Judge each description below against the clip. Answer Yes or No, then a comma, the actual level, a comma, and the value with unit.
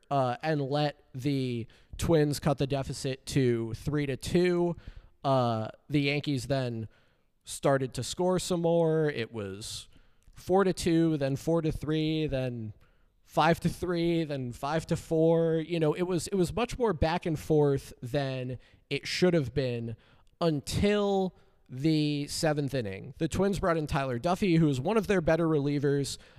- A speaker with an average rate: Yes, average, 160 wpm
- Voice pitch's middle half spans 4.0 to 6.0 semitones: Yes, average, 4.3 semitones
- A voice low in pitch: No, medium, 145 Hz